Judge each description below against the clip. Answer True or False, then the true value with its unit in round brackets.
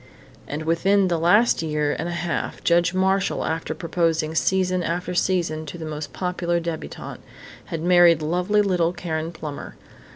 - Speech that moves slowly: False (155 wpm)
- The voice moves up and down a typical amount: False (2.1 semitones)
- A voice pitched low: False (170 Hz)